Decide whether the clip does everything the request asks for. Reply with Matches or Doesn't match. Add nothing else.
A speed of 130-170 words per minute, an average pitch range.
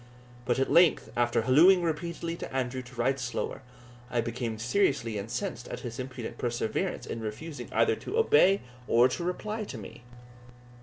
Doesn't match